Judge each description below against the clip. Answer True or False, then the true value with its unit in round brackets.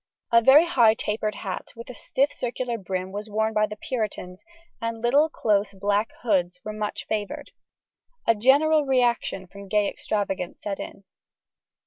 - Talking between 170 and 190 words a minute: False (150 wpm)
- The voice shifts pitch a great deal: False (3.1 semitones)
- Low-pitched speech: False (215 Hz)